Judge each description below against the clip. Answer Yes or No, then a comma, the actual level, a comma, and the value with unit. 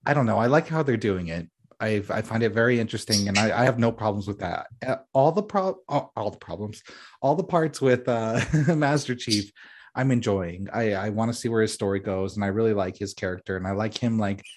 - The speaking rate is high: Yes, fast, 245 wpm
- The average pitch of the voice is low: Yes, low, 110 Hz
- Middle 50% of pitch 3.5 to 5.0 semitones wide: Yes, average, 3.9 semitones